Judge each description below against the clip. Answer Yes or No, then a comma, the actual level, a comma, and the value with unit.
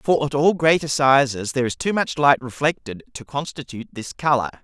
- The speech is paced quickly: No, average, 195 wpm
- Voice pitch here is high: No, medium, 140 Hz